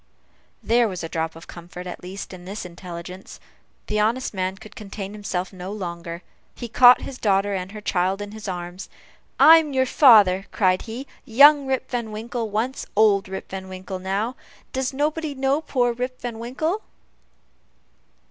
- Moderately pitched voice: No, high, 210 Hz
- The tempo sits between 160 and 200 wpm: Yes, average, 170 wpm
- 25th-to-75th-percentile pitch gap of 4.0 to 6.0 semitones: Yes, average, 5.0 semitones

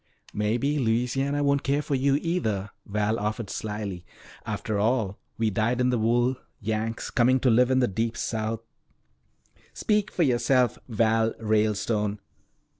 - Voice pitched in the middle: No, low, 115 Hz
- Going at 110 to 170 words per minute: Yes, average, 145 wpm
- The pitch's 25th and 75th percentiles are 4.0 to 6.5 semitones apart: No, average, 3.1 semitones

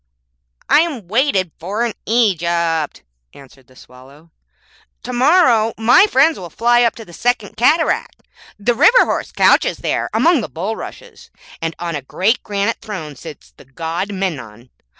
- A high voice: Yes, high, 200 Hz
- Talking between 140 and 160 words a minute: Yes, average, 150 wpm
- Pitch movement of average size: No, wide, 6.8 semitones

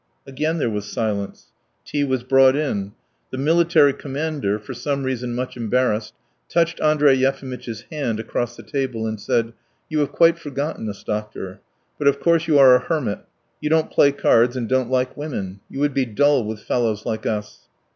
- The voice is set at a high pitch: No, low, 130 Hz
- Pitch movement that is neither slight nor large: Yes, average, 4.5 semitones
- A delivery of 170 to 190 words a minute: Yes, average, 180 wpm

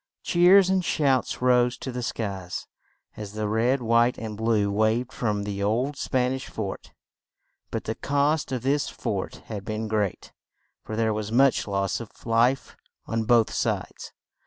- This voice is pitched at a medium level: No, low, 115 Hz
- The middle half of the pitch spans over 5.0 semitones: No, average, 3.3 semitones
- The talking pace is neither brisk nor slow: Yes, average, 160 wpm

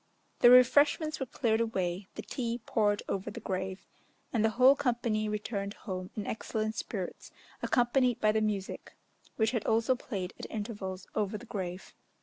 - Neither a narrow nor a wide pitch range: Yes, average, 3.4 semitones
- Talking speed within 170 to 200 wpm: No, average, 160 wpm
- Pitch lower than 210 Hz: No, high, 220 Hz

